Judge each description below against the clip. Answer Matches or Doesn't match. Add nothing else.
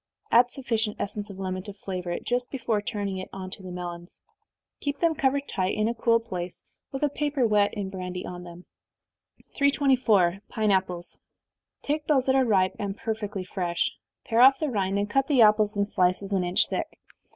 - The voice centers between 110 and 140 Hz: Doesn't match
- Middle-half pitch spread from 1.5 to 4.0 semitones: Doesn't match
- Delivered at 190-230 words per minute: Matches